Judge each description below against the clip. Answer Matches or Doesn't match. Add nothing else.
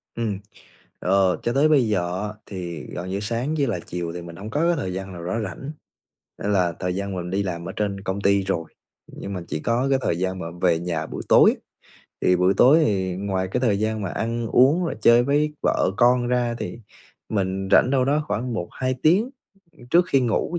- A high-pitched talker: Doesn't match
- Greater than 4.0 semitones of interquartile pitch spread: Matches